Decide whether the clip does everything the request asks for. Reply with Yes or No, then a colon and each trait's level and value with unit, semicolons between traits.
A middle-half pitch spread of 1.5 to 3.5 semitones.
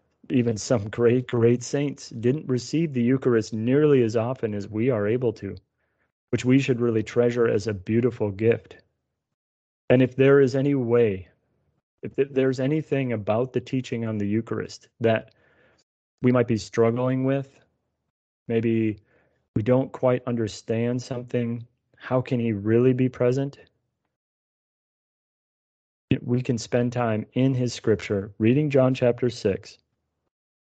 Yes: narrow, 2.6 semitones